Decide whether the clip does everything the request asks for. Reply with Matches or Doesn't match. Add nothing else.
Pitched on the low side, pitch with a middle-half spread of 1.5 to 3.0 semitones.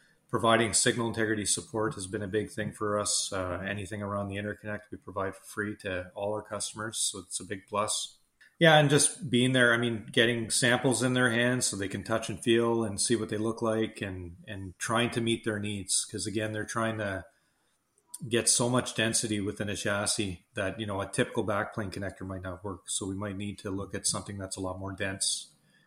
Matches